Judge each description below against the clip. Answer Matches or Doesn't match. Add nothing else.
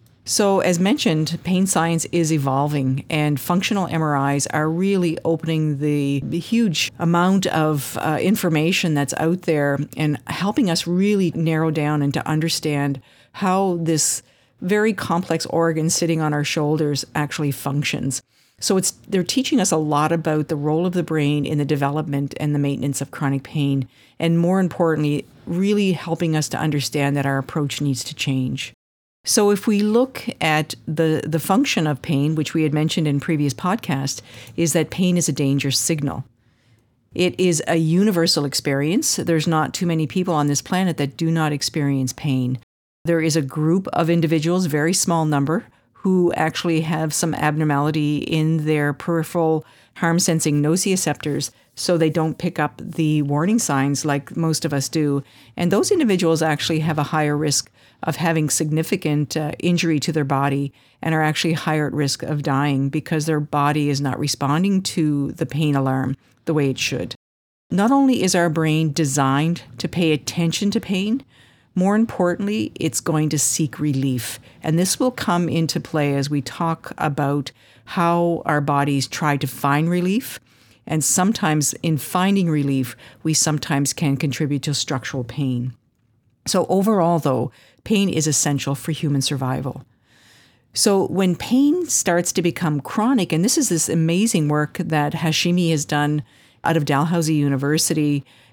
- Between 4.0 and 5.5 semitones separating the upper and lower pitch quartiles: Doesn't match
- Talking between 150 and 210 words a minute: Matches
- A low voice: Doesn't match